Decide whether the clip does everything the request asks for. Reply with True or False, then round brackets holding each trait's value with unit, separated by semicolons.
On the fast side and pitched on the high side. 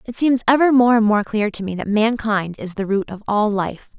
True (255 wpm; 215 Hz)